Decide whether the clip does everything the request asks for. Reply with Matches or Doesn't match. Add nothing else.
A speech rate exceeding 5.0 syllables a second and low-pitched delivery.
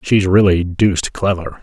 Doesn't match